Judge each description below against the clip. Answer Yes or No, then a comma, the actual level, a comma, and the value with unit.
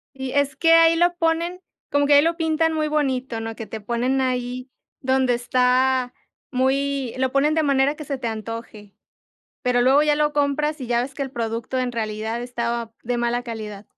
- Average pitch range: Yes, average, 3.5 semitones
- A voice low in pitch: No, very high, 260 Hz